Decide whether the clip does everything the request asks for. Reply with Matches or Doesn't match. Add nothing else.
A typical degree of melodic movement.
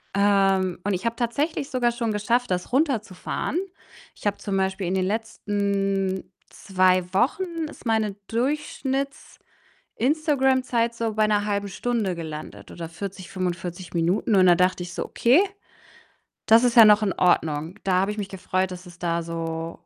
Matches